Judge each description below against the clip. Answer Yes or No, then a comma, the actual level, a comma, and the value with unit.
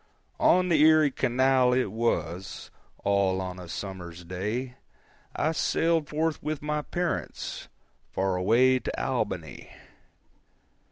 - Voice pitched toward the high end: No, low, 125 Hz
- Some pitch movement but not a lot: No, wide, 8.0 semitones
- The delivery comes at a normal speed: No, slow, 115 wpm